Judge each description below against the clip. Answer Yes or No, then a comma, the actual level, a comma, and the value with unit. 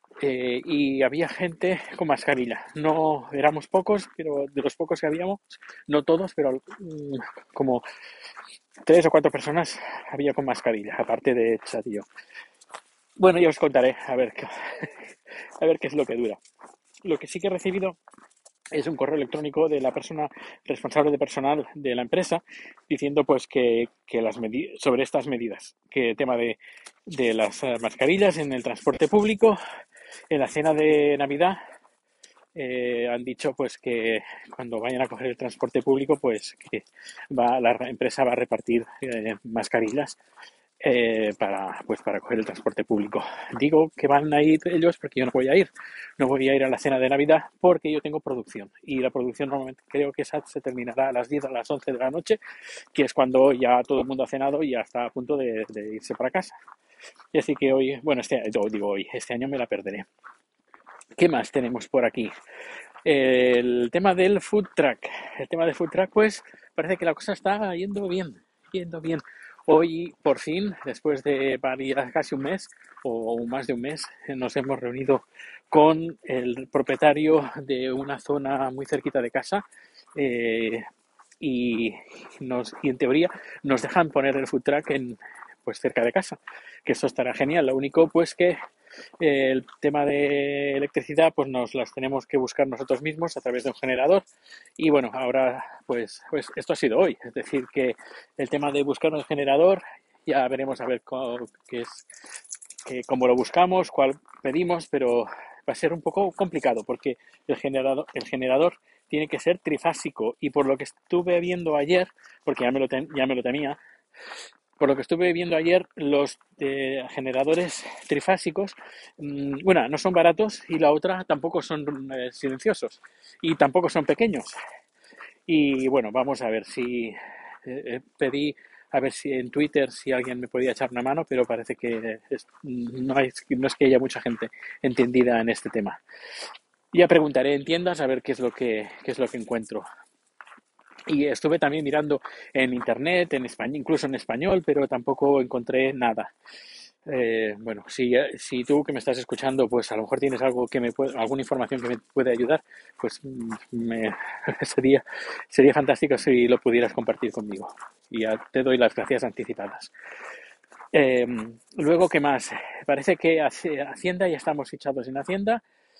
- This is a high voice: No, medium, 140 Hz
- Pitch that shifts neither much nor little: Yes, average, 4.0 semitones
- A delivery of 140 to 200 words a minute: Yes, average, 180 wpm